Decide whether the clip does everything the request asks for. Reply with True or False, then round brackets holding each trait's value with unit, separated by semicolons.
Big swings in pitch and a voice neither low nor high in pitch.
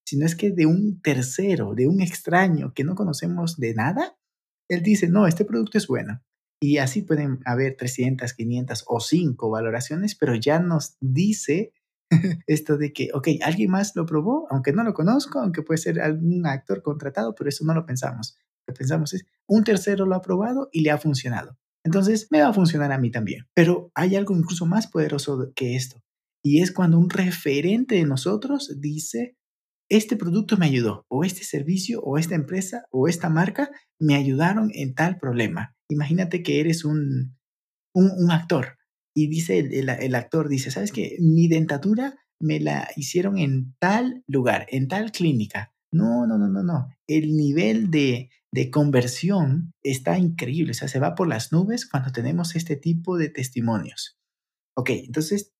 True (5.7 semitones; 160 Hz)